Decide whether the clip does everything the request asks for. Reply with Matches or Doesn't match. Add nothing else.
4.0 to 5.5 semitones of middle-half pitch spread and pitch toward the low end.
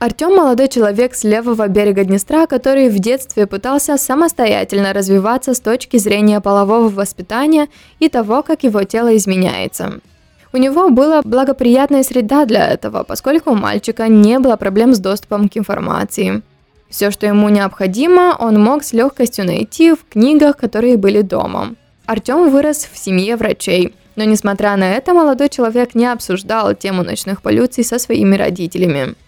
Doesn't match